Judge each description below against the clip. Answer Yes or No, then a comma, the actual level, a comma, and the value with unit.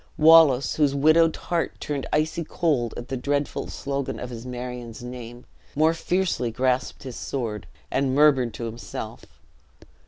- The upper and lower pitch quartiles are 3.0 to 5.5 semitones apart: Yes, average, 3.7 semitones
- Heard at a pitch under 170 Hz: Yes, low, 135 Hz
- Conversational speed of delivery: Yes, average, 145 wpm